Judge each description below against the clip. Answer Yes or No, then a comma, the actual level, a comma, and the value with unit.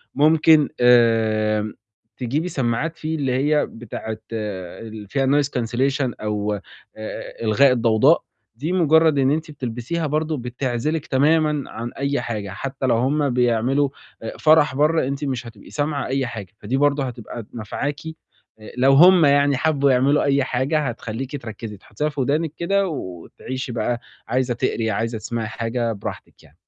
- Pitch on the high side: No, low, 130 Hz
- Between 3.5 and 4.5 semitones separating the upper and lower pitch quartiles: Yes, average, 4.2 semitones